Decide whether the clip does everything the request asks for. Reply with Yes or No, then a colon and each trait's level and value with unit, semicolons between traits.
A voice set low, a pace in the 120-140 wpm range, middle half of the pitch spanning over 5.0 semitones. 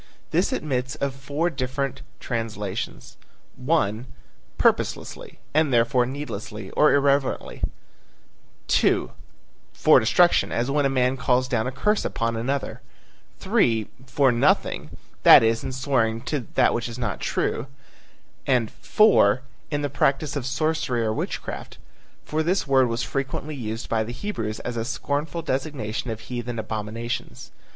No: low, 130 Hz; slow, 135 wpm; average, 3.7 semitones